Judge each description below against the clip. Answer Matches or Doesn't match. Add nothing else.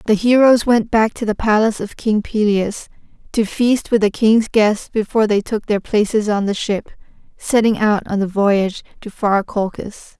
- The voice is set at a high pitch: Matches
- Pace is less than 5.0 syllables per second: Matches